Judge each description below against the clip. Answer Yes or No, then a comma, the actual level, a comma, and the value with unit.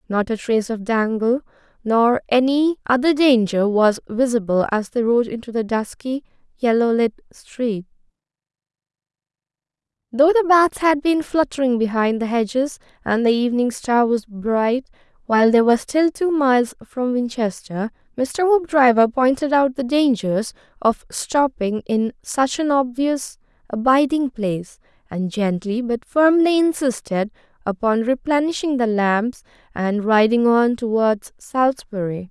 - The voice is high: Yes, high, 245 Hz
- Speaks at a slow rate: Yes, slow, 130 wpm